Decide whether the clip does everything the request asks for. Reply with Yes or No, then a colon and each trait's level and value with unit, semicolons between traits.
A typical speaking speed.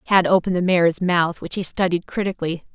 Yes: average, 195 wpm